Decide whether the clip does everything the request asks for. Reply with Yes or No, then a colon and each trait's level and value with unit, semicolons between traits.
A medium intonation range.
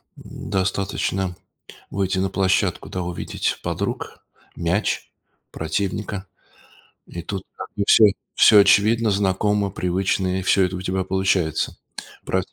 No: narrow, 1.5 semitones